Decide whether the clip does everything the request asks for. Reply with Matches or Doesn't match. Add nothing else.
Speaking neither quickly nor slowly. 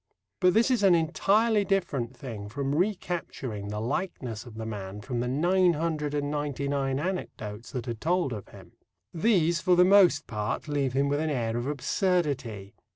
Matches